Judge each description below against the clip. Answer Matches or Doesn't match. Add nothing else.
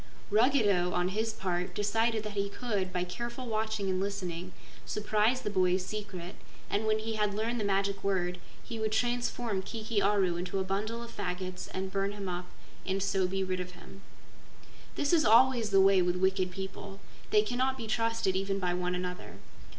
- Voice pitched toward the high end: Matches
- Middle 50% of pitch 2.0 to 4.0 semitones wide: Matches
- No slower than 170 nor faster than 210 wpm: Matches